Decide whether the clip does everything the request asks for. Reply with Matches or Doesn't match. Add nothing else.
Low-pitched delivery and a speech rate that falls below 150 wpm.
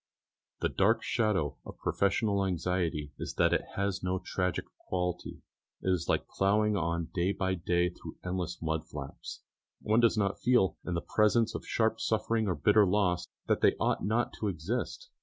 Doesn't match